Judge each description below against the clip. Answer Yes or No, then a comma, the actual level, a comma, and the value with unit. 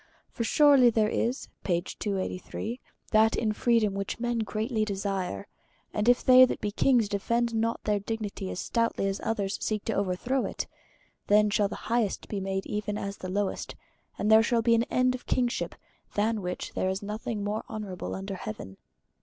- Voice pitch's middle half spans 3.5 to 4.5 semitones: No, average, 2.7 semitones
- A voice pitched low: No, high, 215 Hz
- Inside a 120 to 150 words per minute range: No, average, 175 wpm